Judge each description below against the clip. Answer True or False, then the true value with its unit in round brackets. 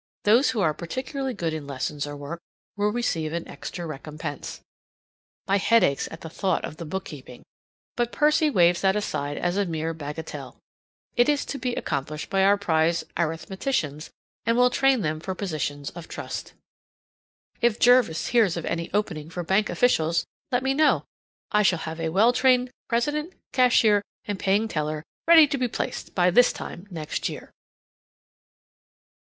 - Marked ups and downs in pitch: True (7.1 semitones)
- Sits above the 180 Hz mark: True (190 Hz)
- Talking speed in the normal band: True (165 wpm)